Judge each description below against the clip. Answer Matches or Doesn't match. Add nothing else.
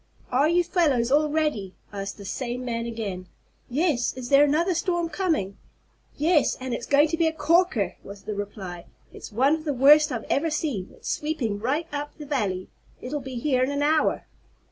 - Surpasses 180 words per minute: Matches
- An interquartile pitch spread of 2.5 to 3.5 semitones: Doesn't match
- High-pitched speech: Matches